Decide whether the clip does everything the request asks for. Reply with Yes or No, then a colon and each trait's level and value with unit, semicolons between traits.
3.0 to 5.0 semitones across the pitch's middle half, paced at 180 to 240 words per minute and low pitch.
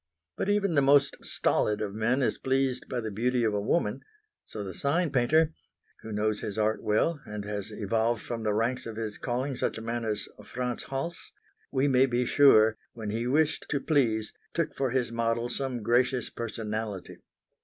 Yes: average, 3.6 semitones; average, 185 wpm; low, 120 Hz